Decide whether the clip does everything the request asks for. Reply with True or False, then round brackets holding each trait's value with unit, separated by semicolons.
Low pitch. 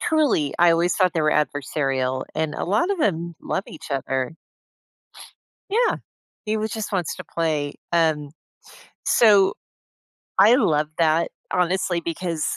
False (170 Hz)